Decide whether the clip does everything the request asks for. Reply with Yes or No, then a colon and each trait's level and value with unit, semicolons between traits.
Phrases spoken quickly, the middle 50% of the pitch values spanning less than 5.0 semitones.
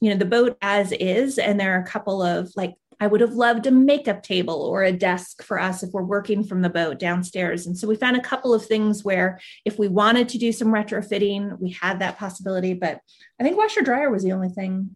Yes: fast, 245 wpm; average, 3.0 semitones